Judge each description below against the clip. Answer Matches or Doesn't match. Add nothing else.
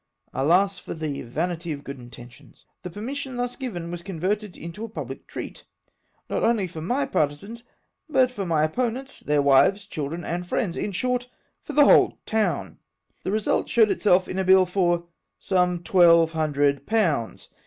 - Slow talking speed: Doesn't match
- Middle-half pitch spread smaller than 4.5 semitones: Doesn't match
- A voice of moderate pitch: Matches